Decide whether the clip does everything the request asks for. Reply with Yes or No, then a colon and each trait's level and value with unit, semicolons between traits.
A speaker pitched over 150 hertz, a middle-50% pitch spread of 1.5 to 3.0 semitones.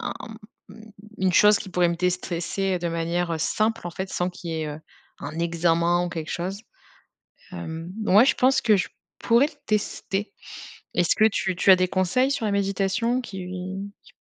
No: medium, 185 Hz; average, 3.5 semitones